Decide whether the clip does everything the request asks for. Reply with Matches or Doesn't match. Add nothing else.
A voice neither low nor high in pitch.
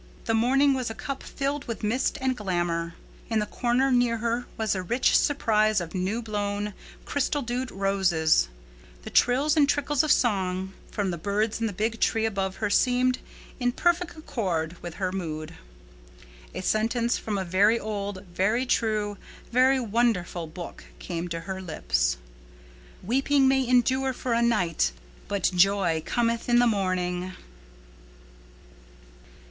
Doesn't match